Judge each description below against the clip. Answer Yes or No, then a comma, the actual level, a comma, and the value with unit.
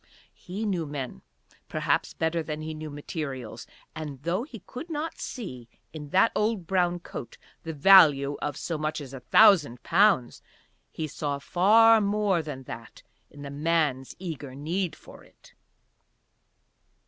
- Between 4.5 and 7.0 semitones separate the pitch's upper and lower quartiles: Yes, average, 5.2 semitones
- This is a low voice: No, medium, 160 Hz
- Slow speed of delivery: No, average, 150 wpm